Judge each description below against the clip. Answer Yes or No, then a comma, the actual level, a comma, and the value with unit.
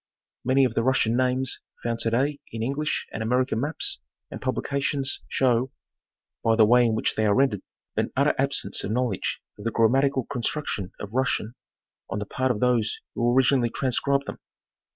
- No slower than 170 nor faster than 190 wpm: Yes, average, 180 wpm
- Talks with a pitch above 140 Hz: No, low, 125 Hz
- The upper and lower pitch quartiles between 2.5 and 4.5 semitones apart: Yes, average, 2.9 semitones